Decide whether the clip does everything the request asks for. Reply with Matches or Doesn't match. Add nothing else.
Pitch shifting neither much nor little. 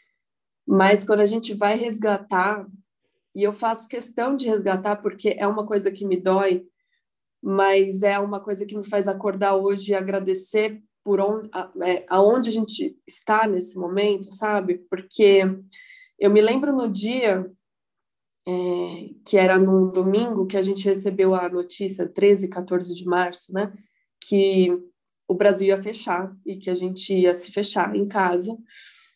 Doesn't match